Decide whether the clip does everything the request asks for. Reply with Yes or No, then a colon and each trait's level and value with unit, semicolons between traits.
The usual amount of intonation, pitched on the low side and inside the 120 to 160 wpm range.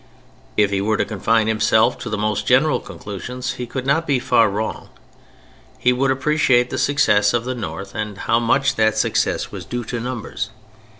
No: average, 3.1 semitones; low, 115 Hz; average, 185 wpm